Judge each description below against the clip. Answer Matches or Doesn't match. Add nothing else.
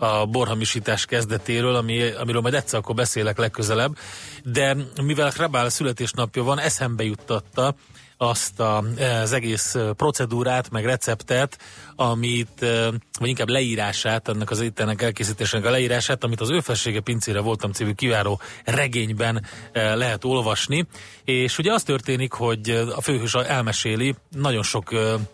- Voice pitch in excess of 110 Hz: Matches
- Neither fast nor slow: Matches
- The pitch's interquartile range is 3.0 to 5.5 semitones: Doesn't match